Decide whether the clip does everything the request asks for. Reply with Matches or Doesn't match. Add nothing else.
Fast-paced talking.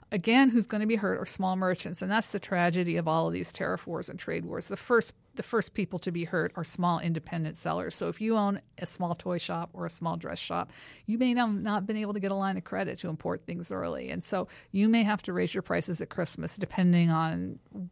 Matches